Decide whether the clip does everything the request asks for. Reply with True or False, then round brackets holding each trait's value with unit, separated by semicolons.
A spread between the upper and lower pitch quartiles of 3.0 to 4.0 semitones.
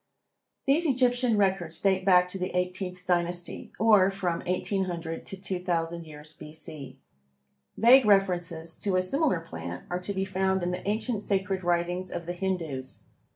False (2.4 semitones)